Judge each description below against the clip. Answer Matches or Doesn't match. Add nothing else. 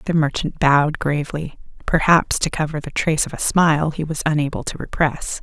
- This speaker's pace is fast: Doesn't match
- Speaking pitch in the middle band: Matches